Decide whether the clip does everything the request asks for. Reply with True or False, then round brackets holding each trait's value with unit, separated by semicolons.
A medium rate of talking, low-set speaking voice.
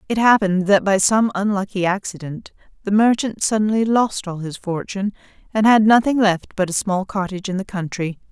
False (180 wpm; 200 Hz)